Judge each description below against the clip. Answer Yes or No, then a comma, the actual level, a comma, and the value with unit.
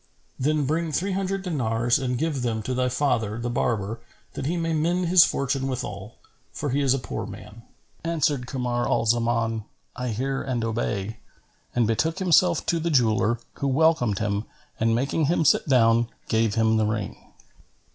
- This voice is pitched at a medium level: No, low, 125 Hz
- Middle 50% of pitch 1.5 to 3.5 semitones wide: No, average, 5.2 semitones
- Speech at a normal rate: Yes, average, 175 wpm